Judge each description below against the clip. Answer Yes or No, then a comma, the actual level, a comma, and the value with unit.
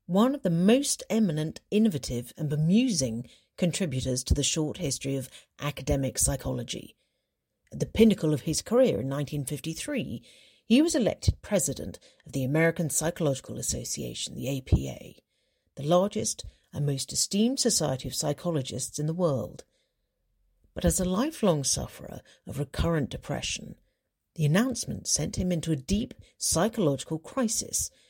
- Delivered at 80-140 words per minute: Yes, slow, 135 wpm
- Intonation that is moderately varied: No, wide, 6.5 semitones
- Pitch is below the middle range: No, medium, 155 Hz